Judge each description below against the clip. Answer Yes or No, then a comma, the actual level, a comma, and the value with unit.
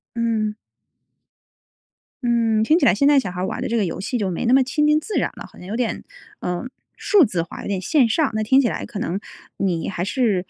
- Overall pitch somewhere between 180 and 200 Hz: No, high, 225 Hz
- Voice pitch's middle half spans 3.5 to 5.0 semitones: No, wide, 5.5 semitones